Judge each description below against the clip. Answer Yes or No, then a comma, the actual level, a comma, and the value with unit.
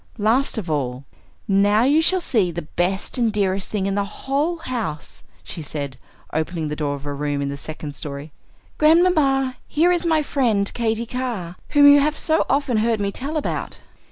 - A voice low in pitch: No, high, 215 Hz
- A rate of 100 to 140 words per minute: No, average, 185 wpm